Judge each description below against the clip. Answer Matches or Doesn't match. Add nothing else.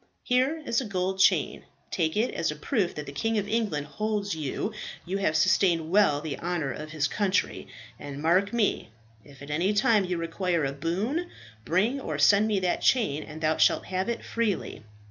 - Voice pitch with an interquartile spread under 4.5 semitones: Doesn't match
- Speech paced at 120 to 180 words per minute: Doesn't match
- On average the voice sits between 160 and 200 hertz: Matches